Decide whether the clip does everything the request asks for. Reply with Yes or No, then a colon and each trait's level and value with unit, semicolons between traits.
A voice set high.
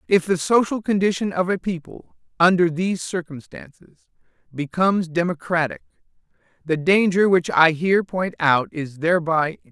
No: medium, 175 Hz